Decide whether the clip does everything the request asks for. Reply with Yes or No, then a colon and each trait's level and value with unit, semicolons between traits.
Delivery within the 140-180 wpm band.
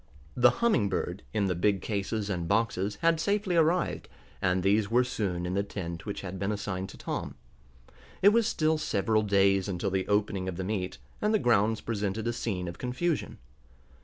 No: average, 190 wpm